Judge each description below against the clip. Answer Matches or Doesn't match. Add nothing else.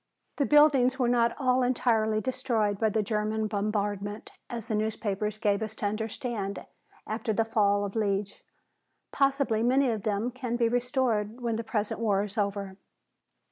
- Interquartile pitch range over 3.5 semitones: Doesn't match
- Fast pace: Doesn't match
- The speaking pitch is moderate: Doesn't match